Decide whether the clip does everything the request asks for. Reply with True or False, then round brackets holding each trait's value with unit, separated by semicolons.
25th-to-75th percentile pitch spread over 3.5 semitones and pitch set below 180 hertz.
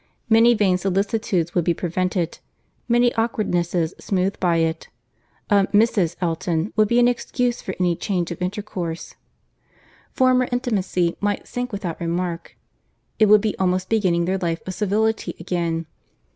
False (4.0 semitones; 185 Hz)